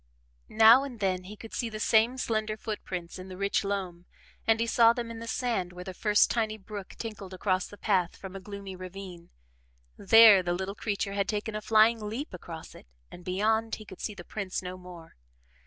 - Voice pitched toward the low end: No, high, 200 Hz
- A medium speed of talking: No, fast, 210 wpm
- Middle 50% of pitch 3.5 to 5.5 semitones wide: No, average, 3.1 semitones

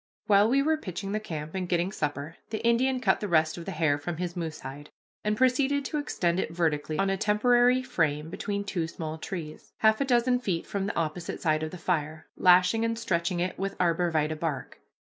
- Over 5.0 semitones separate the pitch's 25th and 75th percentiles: Yes, wide, 5.4 semitones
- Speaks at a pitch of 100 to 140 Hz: No, medium, 180 Hz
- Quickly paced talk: Yes, fast, 215 wpm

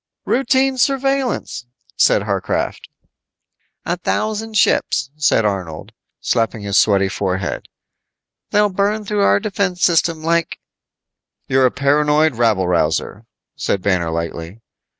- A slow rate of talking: Yes, slow, 115 wpm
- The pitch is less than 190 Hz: Yes, medium, 140 Hz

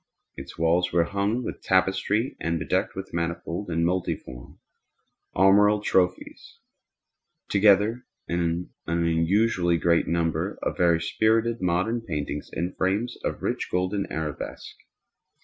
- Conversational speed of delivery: No, slow, 120 wpm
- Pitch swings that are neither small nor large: Yes, average, 3.5 semitones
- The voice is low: Yes, very low, 90 Hz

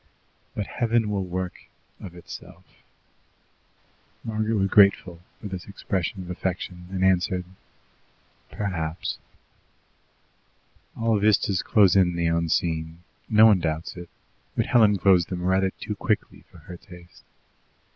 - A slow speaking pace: Yes, slow, 125 wpm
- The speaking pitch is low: Yes, very low, 95 Hz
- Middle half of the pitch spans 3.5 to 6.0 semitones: No, average, 2.8 semitones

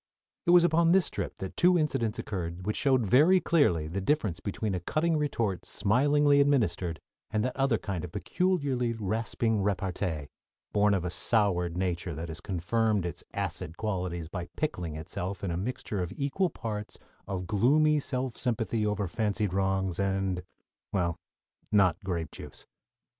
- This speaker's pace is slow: No, average, 160 wpm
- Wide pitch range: Yes, wide, 6.3 semitones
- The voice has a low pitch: Yes, low, 105 Hz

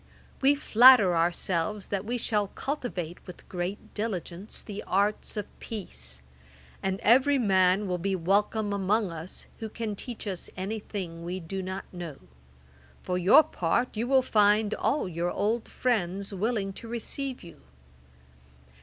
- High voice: Yes, high, 200 Hz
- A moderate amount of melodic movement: Yes, average, 3.7 semitones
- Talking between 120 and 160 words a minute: Yes, average, 145 wpm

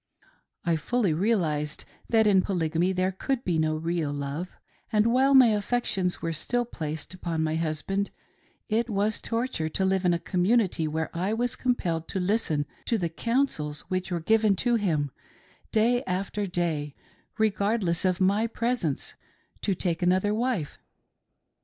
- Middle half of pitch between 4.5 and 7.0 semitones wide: Yes, average, 5.3 semitones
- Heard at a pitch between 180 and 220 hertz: Yes, medium, 185 Hz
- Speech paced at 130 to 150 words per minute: No, average, 160 wpm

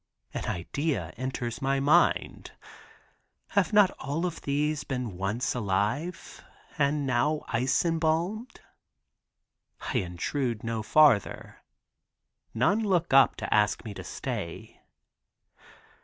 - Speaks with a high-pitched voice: No, low, 135 Hz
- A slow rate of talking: Yes, slow, 105 wpm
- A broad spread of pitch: Yes, wide, 5.8 semitones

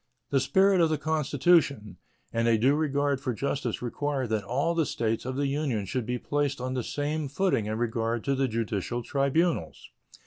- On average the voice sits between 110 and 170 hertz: Yes, low, 135 Hz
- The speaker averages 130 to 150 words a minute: No, average, 185 wpm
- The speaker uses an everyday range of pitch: Yes, average, 4.0 semitones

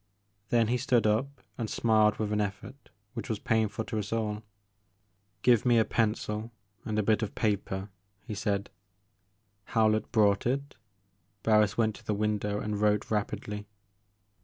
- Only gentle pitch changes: Yes, narrow, 1.5 semitones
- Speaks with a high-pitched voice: No, low, 105 Hz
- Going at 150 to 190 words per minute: Yes, average, 165 wpm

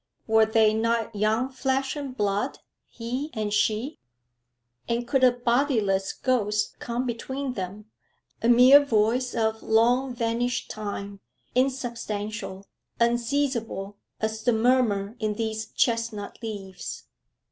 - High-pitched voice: Yes, high, 230 Hz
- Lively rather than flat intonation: No, average, 2.8 semitones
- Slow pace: Yes, slow, 115 wpm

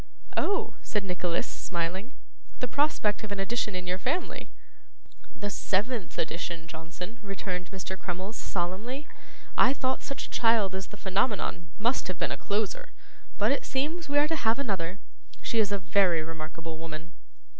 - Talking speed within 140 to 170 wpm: Yes, average, 160 wpm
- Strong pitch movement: No, average, 4.7 semitones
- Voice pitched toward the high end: Yes, high, 195 Hz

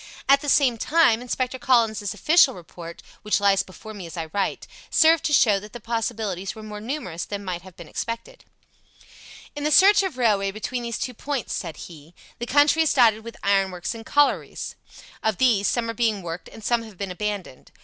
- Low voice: No, high, 220 Hz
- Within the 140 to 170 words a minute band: No, average, 200 wpm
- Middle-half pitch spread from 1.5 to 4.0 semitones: No, average, 4.5 semitones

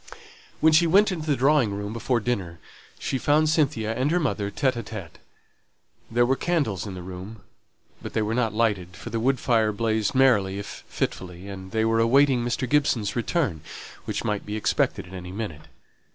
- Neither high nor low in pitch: No, low, 115 Hz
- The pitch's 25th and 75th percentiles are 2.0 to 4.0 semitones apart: No, average, 4.9 semitones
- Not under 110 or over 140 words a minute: No, average, 185 wpm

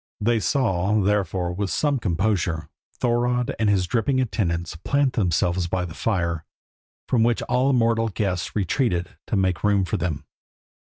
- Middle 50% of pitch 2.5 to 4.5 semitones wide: No, average, 5.0 semitones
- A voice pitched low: Yes, low, 100 Hz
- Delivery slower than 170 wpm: Yes, average, 150 wpm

